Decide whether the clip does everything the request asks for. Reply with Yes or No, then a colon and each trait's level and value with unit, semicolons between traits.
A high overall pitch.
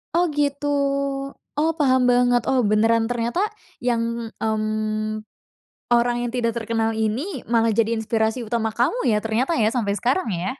Yes: high, 230 Hz